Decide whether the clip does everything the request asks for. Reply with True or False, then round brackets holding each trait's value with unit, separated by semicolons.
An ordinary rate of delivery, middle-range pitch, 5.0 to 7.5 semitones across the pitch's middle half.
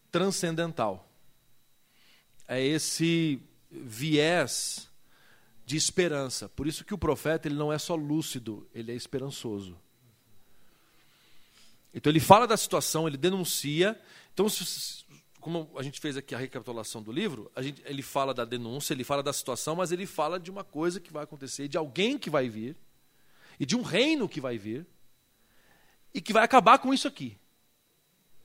True (160 wpm; 150 Hz; 5.3 semitones)